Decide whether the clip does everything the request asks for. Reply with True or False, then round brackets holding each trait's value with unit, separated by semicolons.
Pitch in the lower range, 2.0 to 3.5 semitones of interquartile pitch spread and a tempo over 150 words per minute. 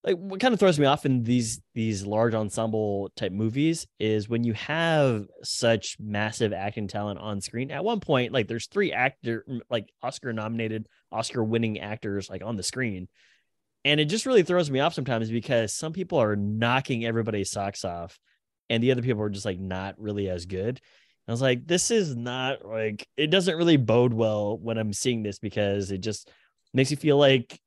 False (115 Hz; 4.0 semitones; 200 wpm)